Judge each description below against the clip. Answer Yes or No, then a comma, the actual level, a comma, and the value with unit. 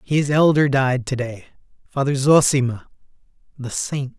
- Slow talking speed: Yes, slow, 130 wpm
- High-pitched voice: No, low, 135 Hz